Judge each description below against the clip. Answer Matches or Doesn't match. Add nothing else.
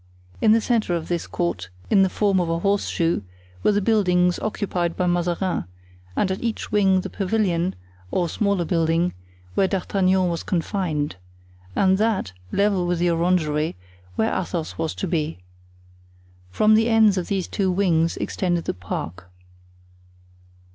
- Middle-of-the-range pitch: Matches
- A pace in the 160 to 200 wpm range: Doesn't match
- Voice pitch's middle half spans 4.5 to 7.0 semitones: Doesn't match